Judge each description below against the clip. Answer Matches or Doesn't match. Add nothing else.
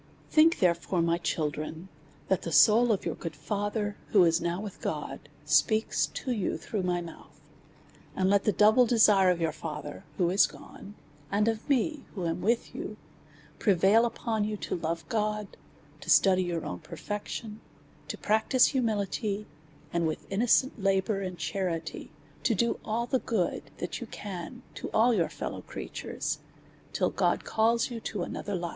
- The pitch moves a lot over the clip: Doesn't match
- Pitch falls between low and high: Doesn't match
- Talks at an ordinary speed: Matches